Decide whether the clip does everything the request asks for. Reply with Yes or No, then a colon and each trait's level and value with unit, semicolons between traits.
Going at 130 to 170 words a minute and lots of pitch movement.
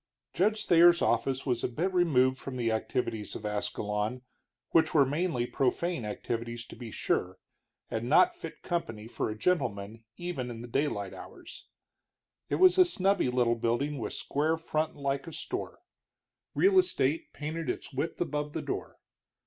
Yes: average, 160 wpm; wide, 6.1 semitones